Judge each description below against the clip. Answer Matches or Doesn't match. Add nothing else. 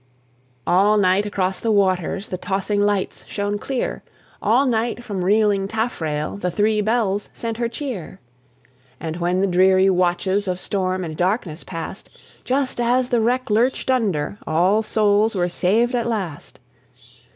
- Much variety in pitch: Doesn't match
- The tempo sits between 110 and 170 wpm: Matches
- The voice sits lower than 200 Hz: Doesn't match